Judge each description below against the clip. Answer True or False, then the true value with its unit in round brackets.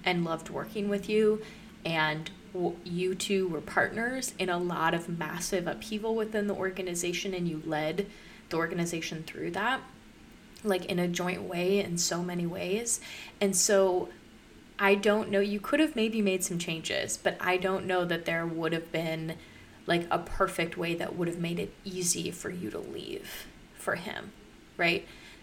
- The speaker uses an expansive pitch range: False (3.0 semitones)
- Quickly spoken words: False (170 wpm)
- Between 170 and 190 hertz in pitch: True (185 Hz)